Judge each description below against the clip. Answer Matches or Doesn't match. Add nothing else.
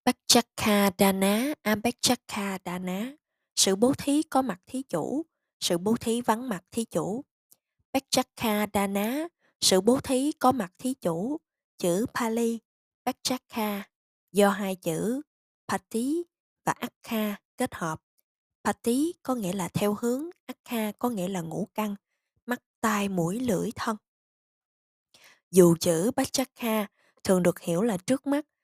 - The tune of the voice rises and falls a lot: Doesn't match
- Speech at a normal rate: Doesn't match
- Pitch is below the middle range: Doesn't match